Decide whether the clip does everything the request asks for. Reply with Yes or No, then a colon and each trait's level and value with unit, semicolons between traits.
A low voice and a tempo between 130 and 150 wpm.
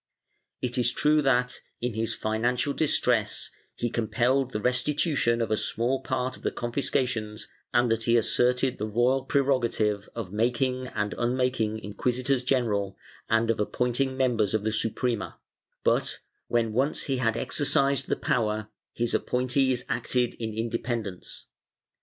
Yes: low, 120 Hz; average, 140 wpm